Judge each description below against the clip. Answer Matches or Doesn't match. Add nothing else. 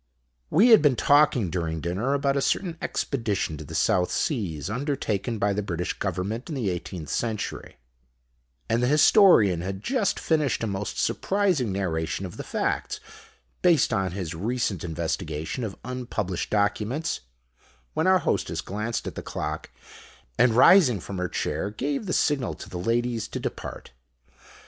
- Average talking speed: Matches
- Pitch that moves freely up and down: Matches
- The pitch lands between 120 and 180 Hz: Doesn't match